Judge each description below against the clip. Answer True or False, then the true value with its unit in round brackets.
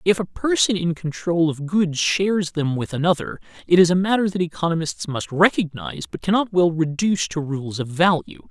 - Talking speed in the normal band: True (190 wpm)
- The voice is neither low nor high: True (165 Hz)